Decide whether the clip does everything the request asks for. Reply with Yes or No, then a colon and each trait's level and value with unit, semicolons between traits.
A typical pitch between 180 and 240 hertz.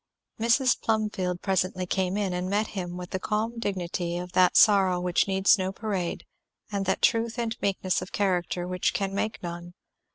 Yes: high, 190 Hz